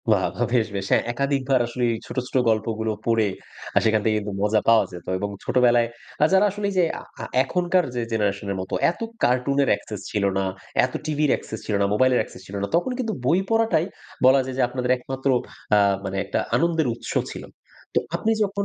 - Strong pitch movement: Yes, wide, 5.8 semitones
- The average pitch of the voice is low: Yes, low, 125 Hz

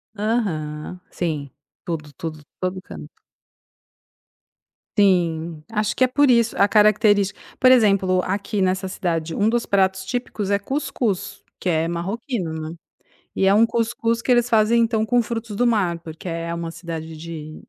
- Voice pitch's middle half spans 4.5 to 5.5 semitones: Yes, average, 5.1 semitones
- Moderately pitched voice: No, high, 195 Hz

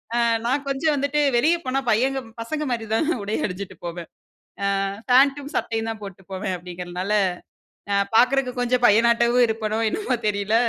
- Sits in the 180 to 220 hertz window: No, high, 230 Hz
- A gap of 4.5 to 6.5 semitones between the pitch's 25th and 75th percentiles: Yes, average, 4.9 semitones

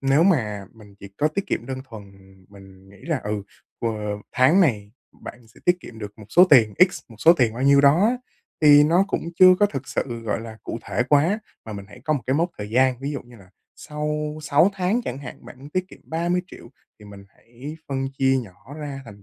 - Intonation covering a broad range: Yes, wide, 5.9 semitones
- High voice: No, low, 135 Hz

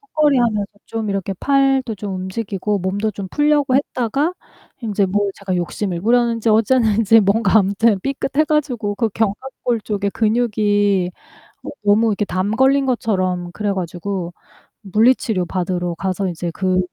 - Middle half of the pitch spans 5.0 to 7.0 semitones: No, average, 3.8 semitones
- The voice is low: No, high, 210 Hz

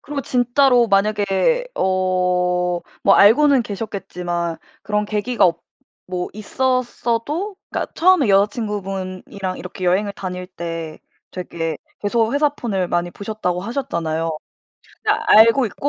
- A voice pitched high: Yes, high, 200 Hz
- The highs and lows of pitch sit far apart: No, average, 4.9 semitones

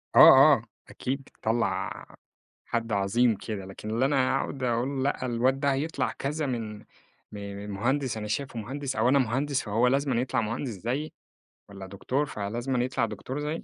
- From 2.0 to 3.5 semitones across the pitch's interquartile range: No, average, 4.0 semitones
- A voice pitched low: Yes, low, 125 Hz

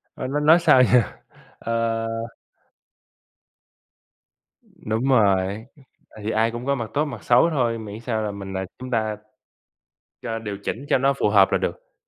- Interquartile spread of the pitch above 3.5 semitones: No, average, 3.2 semitones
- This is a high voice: No, low, 115 Hz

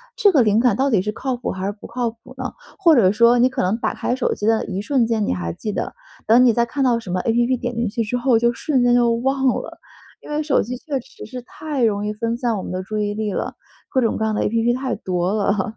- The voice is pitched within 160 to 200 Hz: No, high, 235 Hz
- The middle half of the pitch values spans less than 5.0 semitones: Yes, average, 3.0 semitones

